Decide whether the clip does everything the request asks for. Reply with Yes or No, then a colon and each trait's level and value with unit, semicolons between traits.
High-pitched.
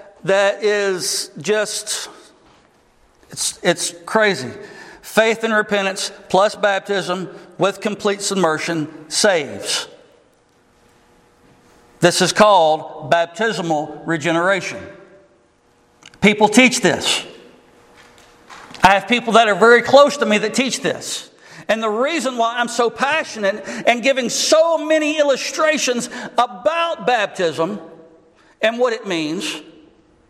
Yes: high, 205 Hz